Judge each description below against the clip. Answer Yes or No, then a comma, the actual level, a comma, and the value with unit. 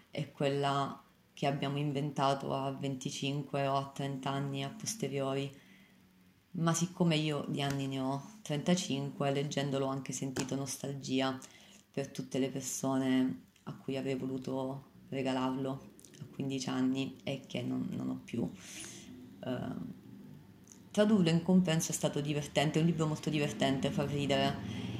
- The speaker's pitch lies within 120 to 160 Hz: Yes, medium, 140 Hz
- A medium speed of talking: Yes, average, 140 wpm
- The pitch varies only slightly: Yes, narrow, 1.5 semitones